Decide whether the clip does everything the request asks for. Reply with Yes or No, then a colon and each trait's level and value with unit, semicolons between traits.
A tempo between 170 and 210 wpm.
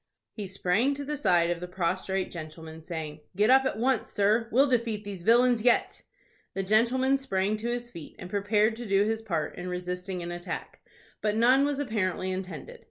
Yes: average, 190 wpm